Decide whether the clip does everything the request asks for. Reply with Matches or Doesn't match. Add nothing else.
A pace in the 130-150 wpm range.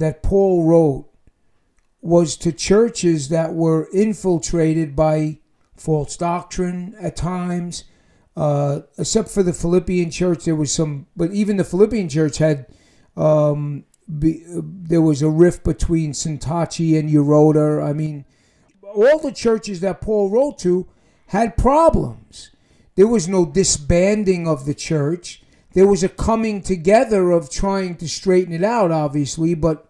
Matches